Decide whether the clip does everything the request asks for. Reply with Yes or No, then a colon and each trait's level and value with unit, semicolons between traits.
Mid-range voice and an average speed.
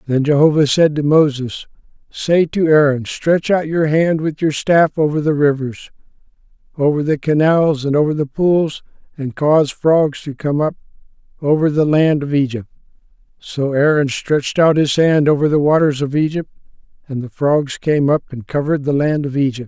Yes: medium, 150 Hz; average, 175 wpm